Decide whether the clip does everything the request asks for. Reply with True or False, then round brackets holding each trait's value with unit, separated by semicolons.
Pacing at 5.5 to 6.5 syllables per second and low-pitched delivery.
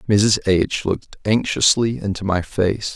False (4.3 syllables/s; 100 Hz)